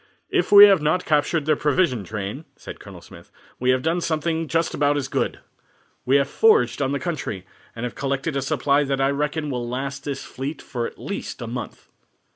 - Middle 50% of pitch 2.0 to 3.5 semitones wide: Yes, average, 3.2 semitones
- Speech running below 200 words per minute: No, fast, 205 wpm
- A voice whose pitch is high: No, medium, 140 Hz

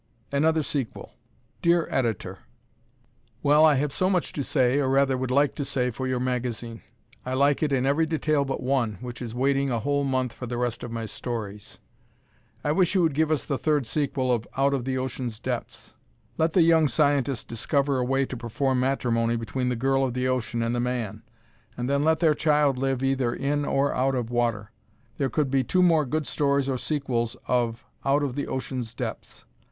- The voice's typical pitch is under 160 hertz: Yes, low, 135 Hz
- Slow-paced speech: No, fast, 205 wpm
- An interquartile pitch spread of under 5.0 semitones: Yes, average, 2.7 semitones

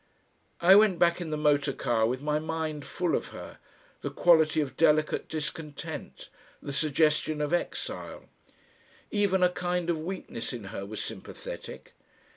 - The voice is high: No, medium, 155 Hz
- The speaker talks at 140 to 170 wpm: Yes, average, 150 wpm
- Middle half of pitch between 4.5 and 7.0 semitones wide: No, average, 2.9 semitones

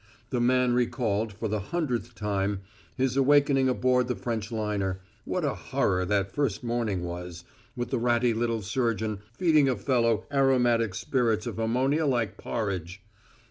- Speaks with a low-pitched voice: Yes, low, 115 Hz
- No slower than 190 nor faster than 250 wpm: No, average, 150 wpm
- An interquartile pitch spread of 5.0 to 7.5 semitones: No, average, 3.5 semitones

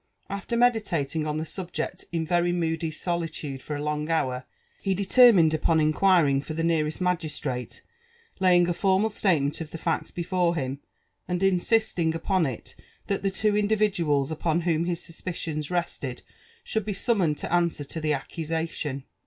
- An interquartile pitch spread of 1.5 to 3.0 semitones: No, average, 3.4 semitones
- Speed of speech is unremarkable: Yes, average, 160 wpm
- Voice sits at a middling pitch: Yes, medium, 165 Hz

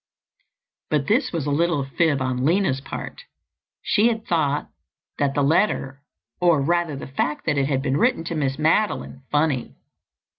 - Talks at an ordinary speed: Yes, average, 160 wpm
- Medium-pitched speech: Yes, medium, 150 Hz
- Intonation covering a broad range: No, average, 3.8 semitones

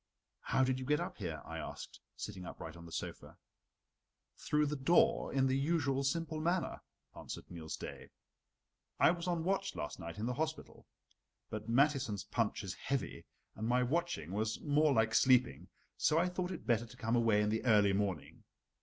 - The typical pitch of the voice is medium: No, low, 125 Hz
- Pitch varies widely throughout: Yes, wide, 6.4 semitones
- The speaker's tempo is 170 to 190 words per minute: Yes, average, 180 wpm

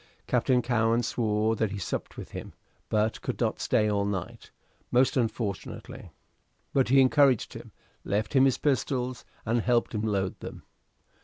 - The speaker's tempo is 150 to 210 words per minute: Yes, average, 155 wpm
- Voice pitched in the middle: No, low, 115 Hz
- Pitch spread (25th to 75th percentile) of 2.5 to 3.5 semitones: Yes, average, 3.0 semitones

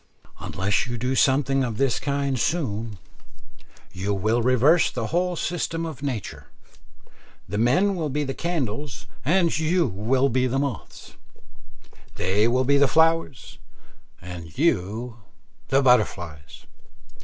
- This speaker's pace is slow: Yes, slow, 120 wpm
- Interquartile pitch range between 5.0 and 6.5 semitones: Yes, wide, 5.4 semitones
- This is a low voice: Yes, low, 130 Hz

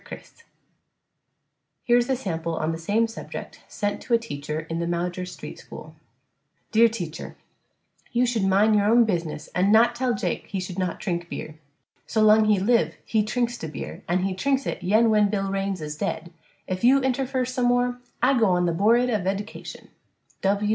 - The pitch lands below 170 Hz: No, high, 210 Hz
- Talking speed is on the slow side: No, average, 190 wpm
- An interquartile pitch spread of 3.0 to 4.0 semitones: No, average, 4.9 semitones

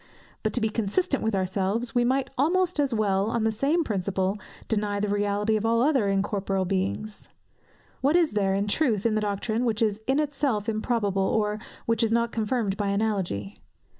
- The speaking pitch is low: No, high, 215 Hz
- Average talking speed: Yes, average, 185 wpm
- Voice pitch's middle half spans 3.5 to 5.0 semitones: No, average, 3.1 semitones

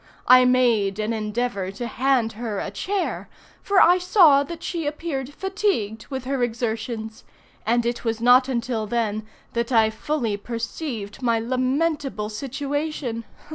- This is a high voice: Yes, high, 240 Hz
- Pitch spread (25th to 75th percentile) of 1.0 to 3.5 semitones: No, average, 4.1 semitones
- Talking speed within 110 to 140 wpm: Yes, slow, 135 wpm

